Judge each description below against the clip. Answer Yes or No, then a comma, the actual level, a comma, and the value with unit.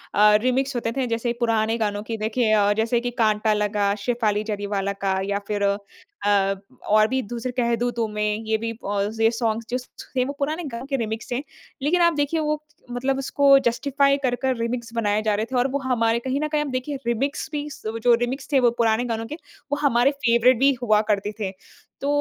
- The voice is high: Yes, high, 235 Hz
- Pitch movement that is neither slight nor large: Yes, average, 3.5 semitones